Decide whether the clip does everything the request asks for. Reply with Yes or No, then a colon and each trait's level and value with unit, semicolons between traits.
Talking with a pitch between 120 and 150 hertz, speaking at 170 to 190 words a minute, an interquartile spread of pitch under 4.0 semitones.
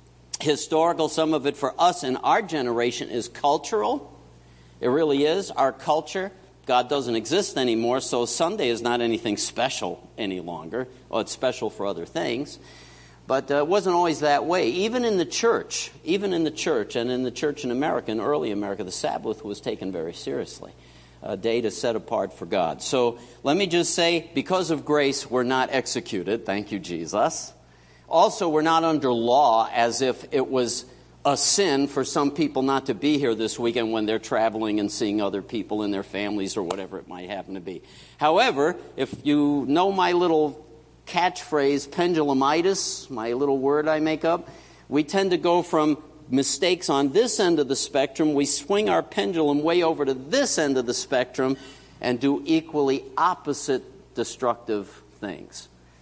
No: low, 135 Hz; average, 180 wpm; average, 5.1 semitones